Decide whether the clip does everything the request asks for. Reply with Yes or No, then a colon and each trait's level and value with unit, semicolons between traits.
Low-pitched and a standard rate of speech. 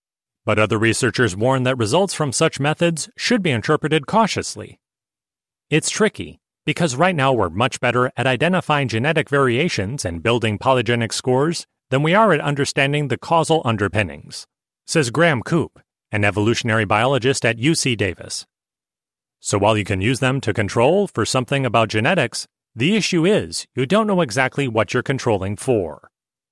Yes: low, 130 Hz; average, 155 wpm